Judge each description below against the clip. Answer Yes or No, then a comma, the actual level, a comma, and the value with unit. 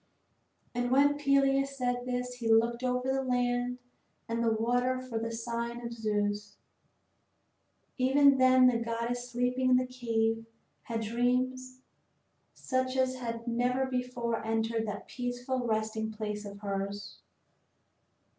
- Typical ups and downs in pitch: No, narrow, 2.2 semitones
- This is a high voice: Yes, high, 245 Hz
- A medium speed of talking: No, slow, 130 wpm